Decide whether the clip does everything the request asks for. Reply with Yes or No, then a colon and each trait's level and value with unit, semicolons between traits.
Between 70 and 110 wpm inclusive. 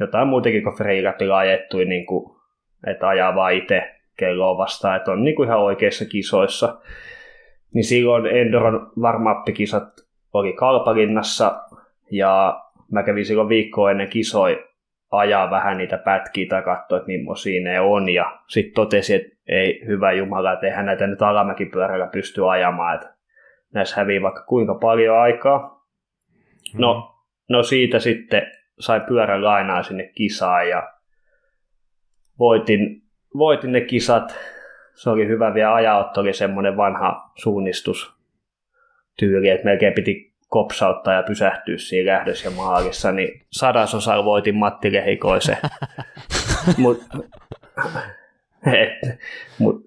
No: average, 125 wpm